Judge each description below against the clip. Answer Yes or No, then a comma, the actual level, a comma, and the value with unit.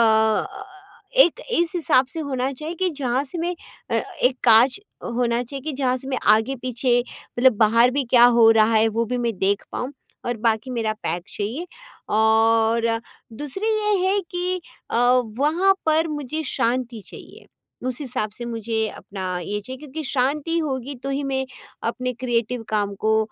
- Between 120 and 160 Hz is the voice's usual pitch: No, very high, 250 Hz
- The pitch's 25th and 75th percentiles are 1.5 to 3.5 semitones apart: No, average, 4.3 semitones